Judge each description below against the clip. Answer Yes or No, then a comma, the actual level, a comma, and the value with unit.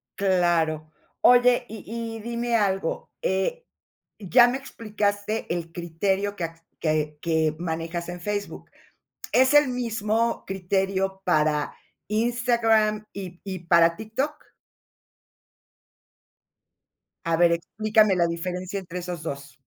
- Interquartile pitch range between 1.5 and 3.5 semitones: No, average, 4.5 semitones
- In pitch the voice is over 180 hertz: Yes, high, 190 Hz